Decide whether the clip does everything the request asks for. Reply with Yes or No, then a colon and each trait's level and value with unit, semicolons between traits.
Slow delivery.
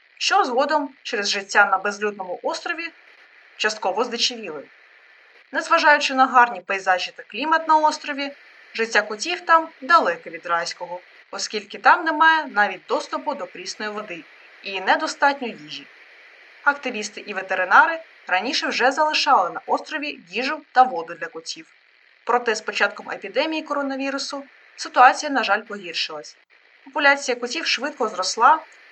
No: average, 125 wpm